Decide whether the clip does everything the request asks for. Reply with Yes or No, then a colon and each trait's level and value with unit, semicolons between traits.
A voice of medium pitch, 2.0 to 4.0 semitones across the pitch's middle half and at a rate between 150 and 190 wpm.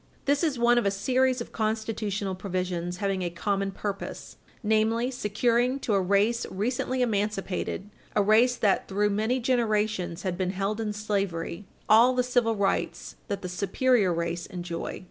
No: high, 210 Hz; average, 3.5 semitones; average, 160 wpm